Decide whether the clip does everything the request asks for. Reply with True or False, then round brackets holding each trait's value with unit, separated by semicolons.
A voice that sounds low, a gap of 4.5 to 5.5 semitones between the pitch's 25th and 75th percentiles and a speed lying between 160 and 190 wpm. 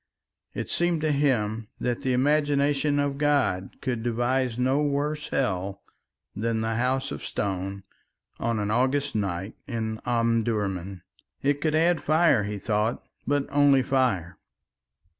False (125 Hz; 5.1 semitones; 135 wpm)